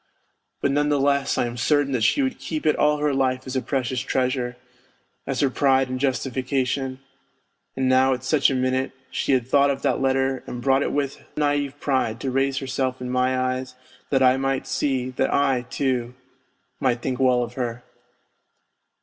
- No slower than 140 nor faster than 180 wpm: No, average, 190 wpm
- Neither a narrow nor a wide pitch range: No, narrow, 1.3 semitones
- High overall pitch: No, low, 130 Hz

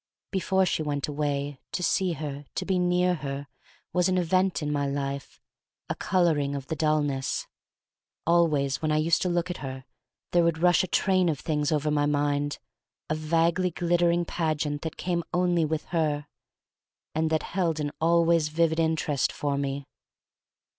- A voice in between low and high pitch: Yes, medium, 155 Hz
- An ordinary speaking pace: Yes, average, 170 wpm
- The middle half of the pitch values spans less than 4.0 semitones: Yes, average, 3.0 semitones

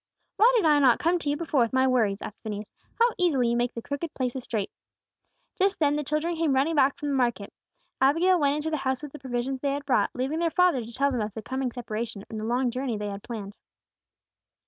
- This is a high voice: Yes, very high, 265 Hz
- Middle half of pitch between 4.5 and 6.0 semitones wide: No, average, 4.1 semitones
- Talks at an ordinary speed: No, fast, 240 wpm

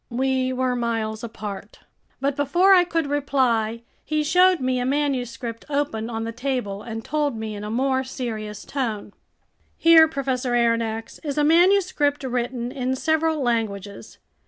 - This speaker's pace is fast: No, average, 150 wpm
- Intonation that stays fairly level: No, average, 4.2 semitones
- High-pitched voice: Yes, very high, 255 Hz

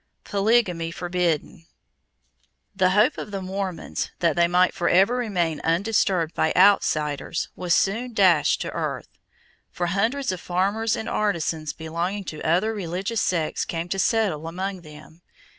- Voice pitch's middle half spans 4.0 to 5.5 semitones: No, average, 3.4 semitones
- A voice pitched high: No, medium, 180 Hz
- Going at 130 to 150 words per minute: Yes, average, 140 wpm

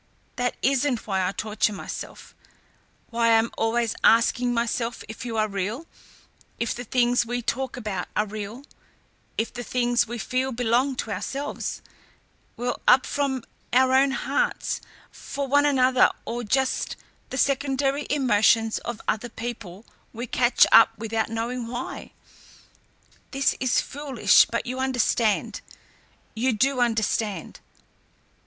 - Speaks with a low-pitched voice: No, high, 240 Hz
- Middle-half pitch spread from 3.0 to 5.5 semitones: No, narrow, 2.6 semitones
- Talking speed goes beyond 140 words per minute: No, slow, 135 wpm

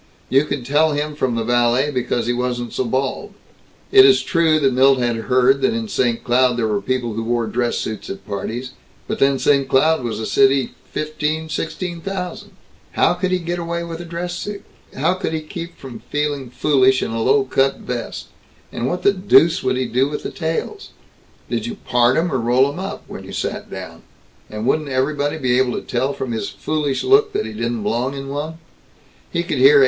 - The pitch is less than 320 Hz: Yes, low, 135 Hz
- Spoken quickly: Yes, fast, 215 wpm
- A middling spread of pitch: Yes, average, 4.7 semitones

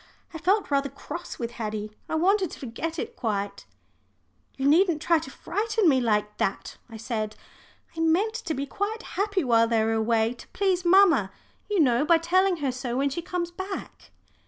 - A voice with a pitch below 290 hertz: No, very high, 305 Hz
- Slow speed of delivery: No, average, 185 wpm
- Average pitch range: No, wide, 8.0 semitones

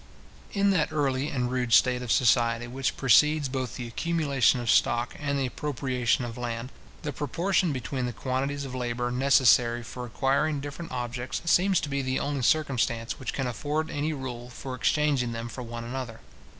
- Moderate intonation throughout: Yes, average, 3.0 semitones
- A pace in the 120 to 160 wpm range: No, average, 175 wpm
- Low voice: Yes, low, 130 Hz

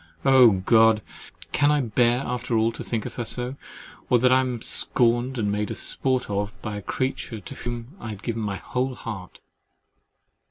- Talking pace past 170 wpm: Yes, average, 190 wpm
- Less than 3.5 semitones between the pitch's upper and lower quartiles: Yes, average, 2.8 semitones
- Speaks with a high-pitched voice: No, low, 120 Hz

